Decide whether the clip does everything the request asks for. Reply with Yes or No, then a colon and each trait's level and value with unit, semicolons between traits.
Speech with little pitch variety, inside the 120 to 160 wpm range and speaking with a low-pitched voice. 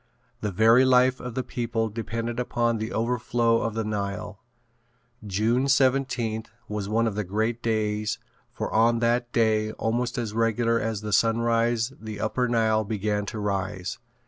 Yes: narrow, 1.7 semitones; average, 155 wpm; low, 115 Hz